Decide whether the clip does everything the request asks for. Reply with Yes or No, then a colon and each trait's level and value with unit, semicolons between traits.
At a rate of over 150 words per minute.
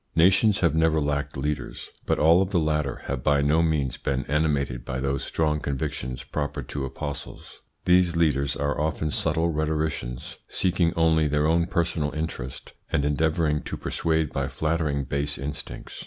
Yes: average, 160 wpm